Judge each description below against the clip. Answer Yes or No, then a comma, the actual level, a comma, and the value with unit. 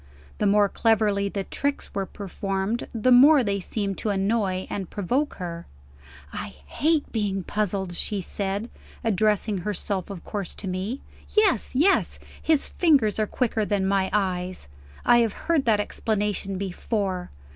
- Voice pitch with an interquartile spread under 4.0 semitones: Yes, average, 2.8 semitones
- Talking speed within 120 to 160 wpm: Yes, average, 145 wpm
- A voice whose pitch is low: No, high, 205 Hz